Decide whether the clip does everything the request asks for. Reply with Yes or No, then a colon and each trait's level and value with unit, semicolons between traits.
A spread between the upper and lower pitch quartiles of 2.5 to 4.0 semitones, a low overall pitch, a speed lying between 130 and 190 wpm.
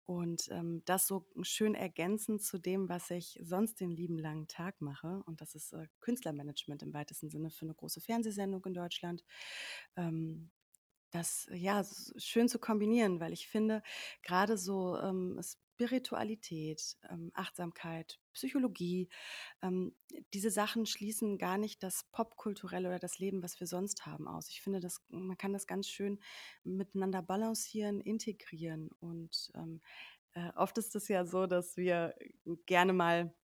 No: average, 3.5 semitones; medium, 185 Hz; average, 155 wpm